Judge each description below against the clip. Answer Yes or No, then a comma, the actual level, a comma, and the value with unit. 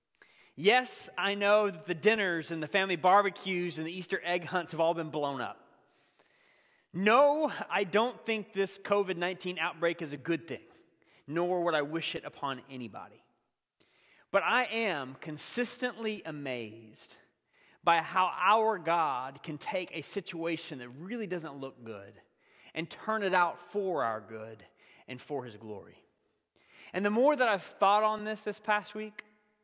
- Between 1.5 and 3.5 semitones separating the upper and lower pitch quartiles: No, average, 5.1 semitones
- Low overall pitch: No, medium, 180 Hz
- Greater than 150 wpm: Yes, average, 160 wpm